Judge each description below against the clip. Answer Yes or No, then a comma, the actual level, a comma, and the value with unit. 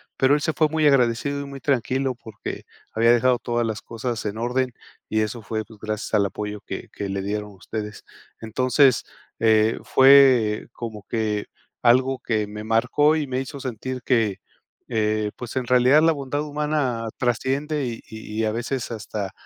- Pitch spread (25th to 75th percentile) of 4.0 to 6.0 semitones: No, average, 3.6 semitones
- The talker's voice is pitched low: Yes, low, 120 Hz